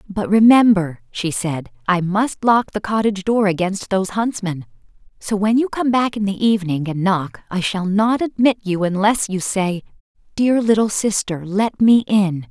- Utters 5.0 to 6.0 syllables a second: No, 4.6 syllables/s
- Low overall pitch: No, high, 200 Hz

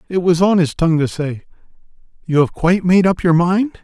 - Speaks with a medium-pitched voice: Yes, medium, 175 Hz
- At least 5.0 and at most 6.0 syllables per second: Yes, 5.8 syllables/s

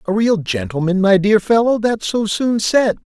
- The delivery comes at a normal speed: Yes, average, 175 wpm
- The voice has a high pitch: Yes, high, 215 Hz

